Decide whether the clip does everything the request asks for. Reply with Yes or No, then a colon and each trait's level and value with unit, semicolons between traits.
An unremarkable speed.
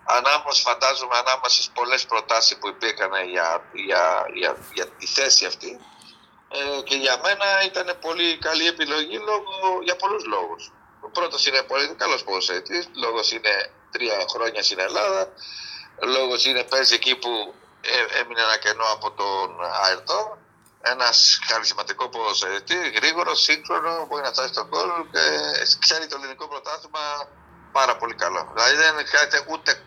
Yes: average, 145 wpm